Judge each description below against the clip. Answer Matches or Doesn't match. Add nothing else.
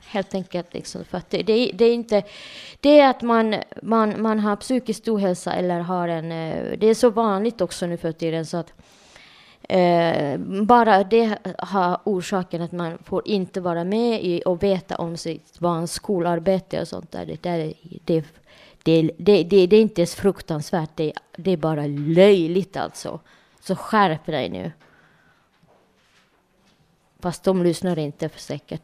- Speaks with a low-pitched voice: Doesn't match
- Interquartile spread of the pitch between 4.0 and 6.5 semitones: Doesn't match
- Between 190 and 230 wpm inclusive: Doesn't match